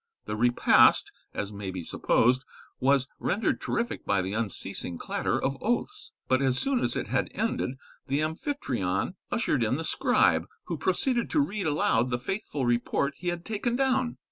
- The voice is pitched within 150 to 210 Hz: No, medium, 140 Hz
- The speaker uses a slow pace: No, average, 170 wpm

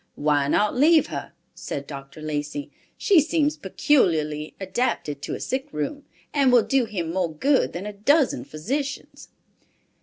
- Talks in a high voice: Yes, high, 195 Hz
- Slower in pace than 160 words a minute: Yes, average, 150 wpm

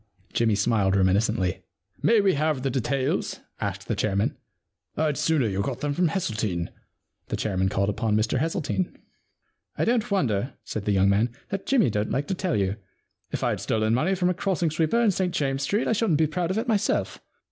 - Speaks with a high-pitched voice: No, low, 135 Hz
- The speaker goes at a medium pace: No, fast, 210 wpm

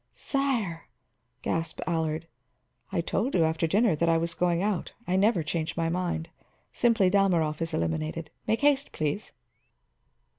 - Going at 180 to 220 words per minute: No, average, 145 wpm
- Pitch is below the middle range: No, medium, 170 Hz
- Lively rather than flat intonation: No, average, 3.8 semitones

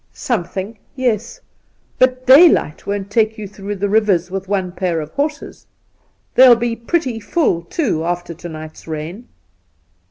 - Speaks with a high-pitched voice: Yes, high, 205 Hz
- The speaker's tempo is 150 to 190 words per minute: Yes, average, 155 wpm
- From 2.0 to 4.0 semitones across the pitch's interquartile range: No, wide, 5.5 semitones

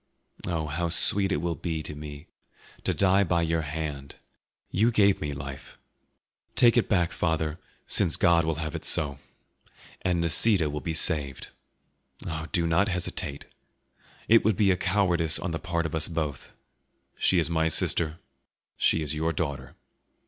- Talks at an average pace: Yes, average, 165 wpm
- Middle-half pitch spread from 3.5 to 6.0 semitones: No, average, 2.8 semitones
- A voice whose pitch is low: Yes, very low, 80 Hz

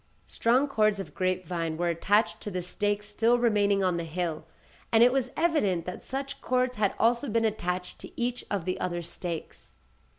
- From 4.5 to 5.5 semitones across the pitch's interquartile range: Yes, average, 4.9 semitones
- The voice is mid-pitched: No, high, 205 Hz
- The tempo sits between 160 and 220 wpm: Yes, average, 190 wpm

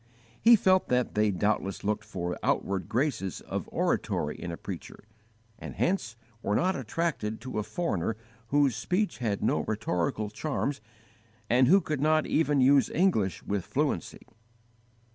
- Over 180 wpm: No, average, 145 wpm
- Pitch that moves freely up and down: Yes, wide, 7.2 semitones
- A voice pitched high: No, low, 120 Hz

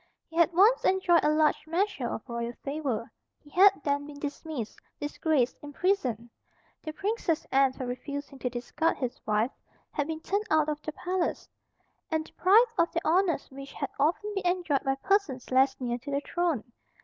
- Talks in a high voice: Yes, very high, 300 Hz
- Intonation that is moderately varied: Yes, average, 4.7 semitones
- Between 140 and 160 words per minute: No, average, 175 wpm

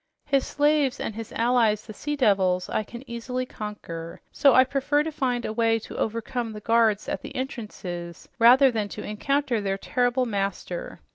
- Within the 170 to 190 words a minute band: Yes, average, 180 wpm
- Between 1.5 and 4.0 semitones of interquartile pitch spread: Yes, average, 3.7 semitones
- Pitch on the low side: No, high, 230 Hz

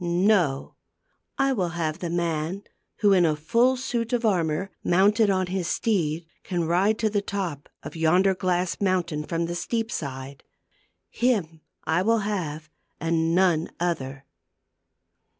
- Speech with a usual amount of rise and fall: Yes, average, 3.9 semitones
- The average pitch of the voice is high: No, medium, 175 Hz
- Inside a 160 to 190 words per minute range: No, average, 145 wpm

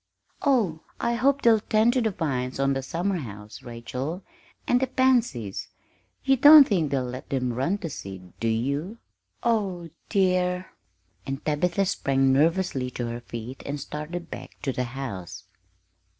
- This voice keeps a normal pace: Yes, average, 150 wpm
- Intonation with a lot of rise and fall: Yes, wide, 7.9 semitones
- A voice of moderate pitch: Yes, medium, 150 Hz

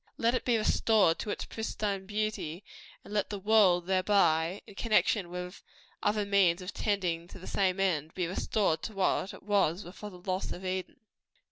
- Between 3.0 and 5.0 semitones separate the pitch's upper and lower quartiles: No, narrow, 2.6 semitones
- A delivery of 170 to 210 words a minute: Yes, average, 175 wpm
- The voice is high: Yes, high, 195 Hz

